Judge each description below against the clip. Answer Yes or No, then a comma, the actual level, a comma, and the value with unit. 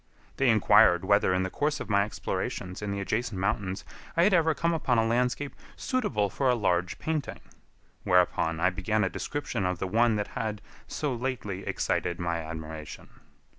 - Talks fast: No, average, 175 wpm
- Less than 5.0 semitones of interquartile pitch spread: No, wide, 5.4 semitones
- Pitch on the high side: No, low, 105 Hz